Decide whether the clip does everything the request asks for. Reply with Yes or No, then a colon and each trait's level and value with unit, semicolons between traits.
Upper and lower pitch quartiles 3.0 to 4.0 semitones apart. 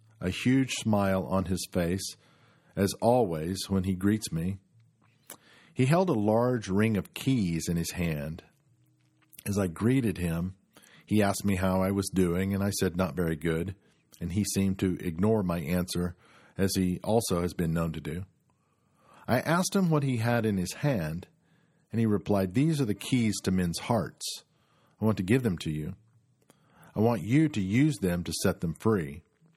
No: average, 4.9 semitones